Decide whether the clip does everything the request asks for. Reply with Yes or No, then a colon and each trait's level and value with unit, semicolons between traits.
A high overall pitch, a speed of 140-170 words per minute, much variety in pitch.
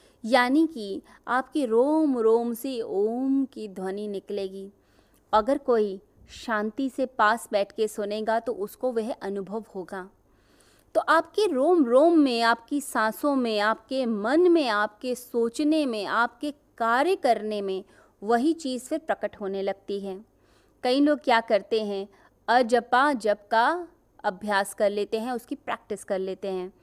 No: high, 230 Hz; average, 145 wpm; average, 4.5 semitones